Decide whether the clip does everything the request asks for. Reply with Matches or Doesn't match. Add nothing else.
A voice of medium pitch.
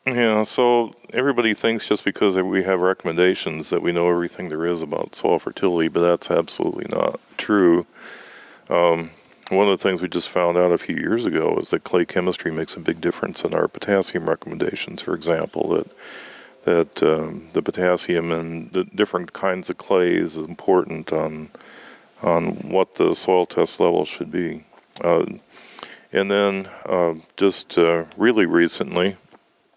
Doesn't match